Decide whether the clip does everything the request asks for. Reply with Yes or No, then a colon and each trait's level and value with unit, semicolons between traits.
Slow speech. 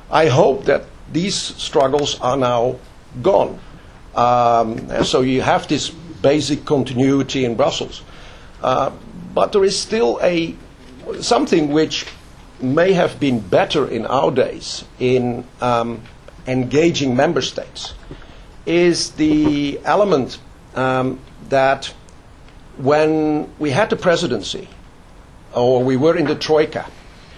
Yes: slow, 120 wpm